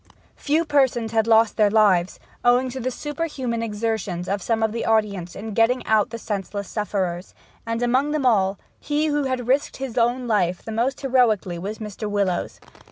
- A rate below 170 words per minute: No, average, 180 wpm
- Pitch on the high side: Yes, high, 225 Hz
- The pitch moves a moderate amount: Yes, average, 3.8 semitones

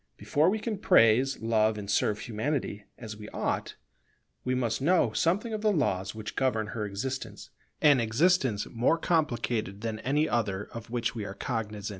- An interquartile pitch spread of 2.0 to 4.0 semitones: No, average, 5.3 semitones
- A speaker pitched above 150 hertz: No, low, 115 Hz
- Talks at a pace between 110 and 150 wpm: No, average, 170 wpm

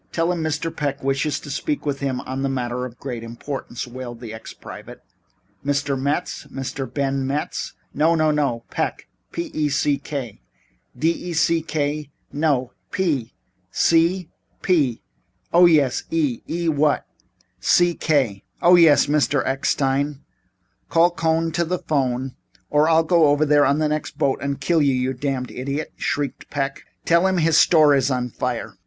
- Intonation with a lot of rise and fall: No, average, 3.4 semitones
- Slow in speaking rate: No, average, 170 wpm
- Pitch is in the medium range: Yes, medium, 145 Hz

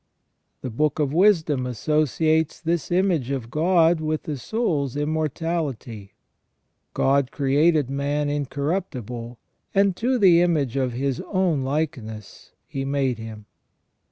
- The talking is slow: Yes, slow, 130 wpm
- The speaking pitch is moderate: Yes, medium, 145 Hz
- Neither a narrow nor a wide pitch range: Yes, average, 3.8 semitones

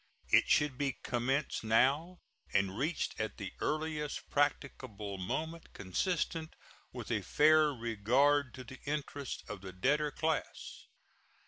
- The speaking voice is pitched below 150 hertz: Yes, medium, 140 Hz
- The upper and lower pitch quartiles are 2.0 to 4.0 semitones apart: No, average, 5.1 semitones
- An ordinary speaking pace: No, slow, 125 wpm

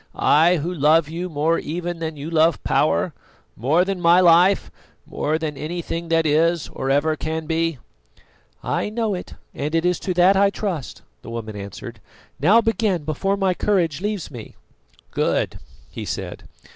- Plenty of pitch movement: No, average, 2.9 semitones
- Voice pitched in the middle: Yes, medium, 165 Hz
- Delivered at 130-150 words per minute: No, average, 165 wpm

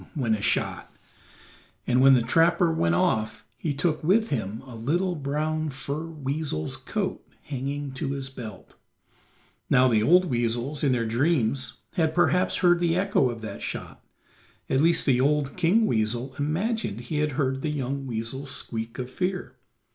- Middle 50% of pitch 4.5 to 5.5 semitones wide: Yes, average, 4.8 semitones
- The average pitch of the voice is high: No, medium, 140 Hz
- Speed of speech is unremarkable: Yes, average, 160 wpm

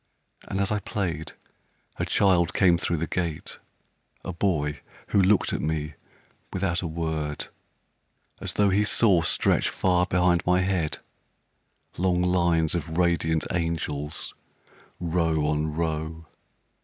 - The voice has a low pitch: Yes, very low, 85 Hz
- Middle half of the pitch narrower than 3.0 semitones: Yes, narrow, 2.4 semitones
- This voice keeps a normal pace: No, slow, 130 wpm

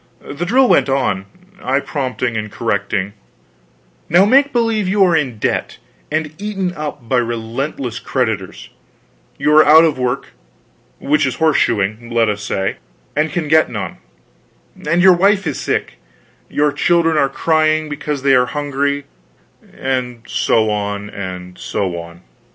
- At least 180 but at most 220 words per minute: No, average, 150 wpm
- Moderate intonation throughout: No, wide, 5.7 semitones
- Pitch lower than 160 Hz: Yes, medium, 140 Hz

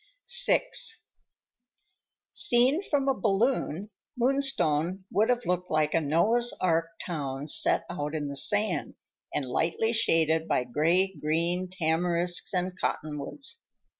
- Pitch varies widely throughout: Yes, wide, 6.0 semitones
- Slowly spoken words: Yes, slow, 120 wpm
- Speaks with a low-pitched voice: No, medium, 175 Hz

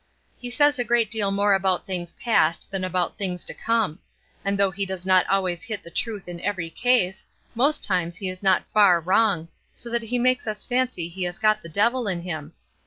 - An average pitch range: Yes, average, 4.2 semitones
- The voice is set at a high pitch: Yes, high, 195 Hz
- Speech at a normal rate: No, fast, 215 wpm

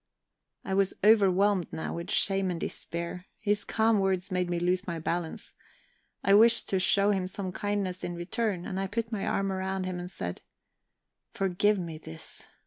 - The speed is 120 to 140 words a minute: No, average, 175 wpm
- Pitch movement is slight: Yes, narrow, 2.2 semitones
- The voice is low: No, high, 190 Hz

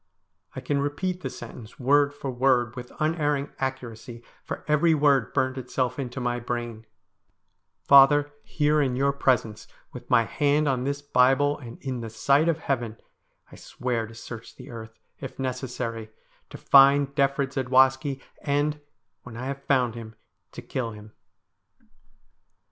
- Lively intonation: No, average, 2.9 semitones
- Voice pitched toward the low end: Yes, low, 130 Hz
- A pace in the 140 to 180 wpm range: Yes, average, 155 wpm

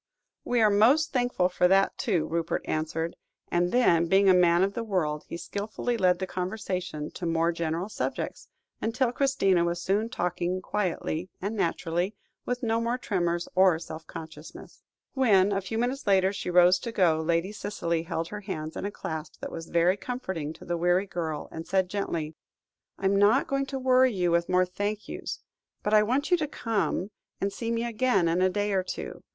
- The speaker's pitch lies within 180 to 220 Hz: Yes, high, 190 Hz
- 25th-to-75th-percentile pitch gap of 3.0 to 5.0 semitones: Yes, average, 4.1 semitones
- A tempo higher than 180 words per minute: Yes, average, 195 wpm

